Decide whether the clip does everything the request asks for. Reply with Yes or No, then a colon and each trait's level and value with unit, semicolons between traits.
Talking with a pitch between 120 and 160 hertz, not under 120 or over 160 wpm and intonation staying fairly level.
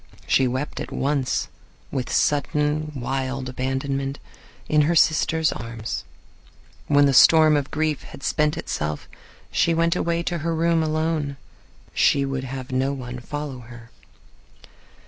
No: medium, 140 Hz; slow, 135 wpm; average, 3.0 semitones